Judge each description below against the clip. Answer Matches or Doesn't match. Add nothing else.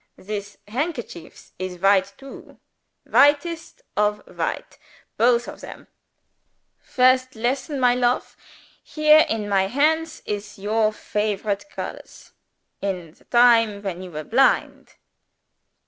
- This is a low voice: Doesn't match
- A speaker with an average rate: Doesn't match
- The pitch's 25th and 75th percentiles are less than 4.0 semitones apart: Doesn't match